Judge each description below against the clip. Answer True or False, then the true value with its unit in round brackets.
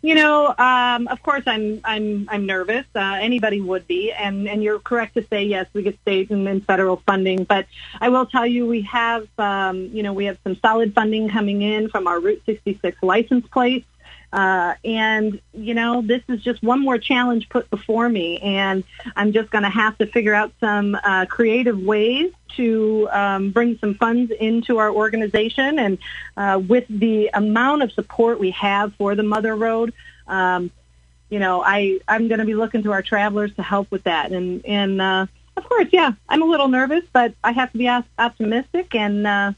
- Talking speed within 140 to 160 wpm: False (200 wpm)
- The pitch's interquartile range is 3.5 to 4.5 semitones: False (3.0 semitones)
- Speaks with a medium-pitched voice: False (215 Hz)